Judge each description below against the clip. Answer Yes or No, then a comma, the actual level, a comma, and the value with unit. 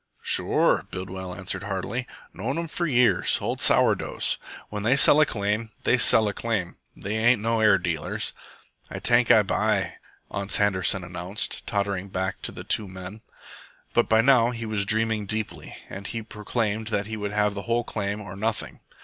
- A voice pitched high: No, low, 105 Hz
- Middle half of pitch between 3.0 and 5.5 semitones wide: No, narrow, 2.5 semitones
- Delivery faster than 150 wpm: Yes, average, 175 wpm